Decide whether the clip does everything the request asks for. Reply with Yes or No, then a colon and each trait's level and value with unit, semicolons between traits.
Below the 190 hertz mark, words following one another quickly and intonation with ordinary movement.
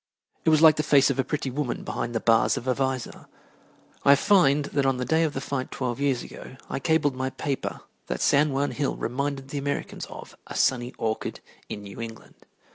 No: low, 135 Hz; fast, 210 wpm; narrow, 2.3 semitones